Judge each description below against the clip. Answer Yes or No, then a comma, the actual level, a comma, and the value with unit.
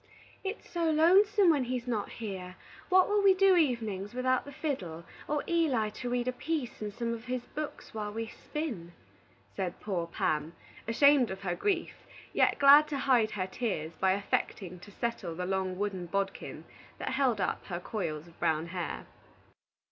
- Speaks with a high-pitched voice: Yes, high, 230 Hz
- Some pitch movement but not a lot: No, wide, 7.2 semitones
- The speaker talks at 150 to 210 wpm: Yes, average, 175 wpm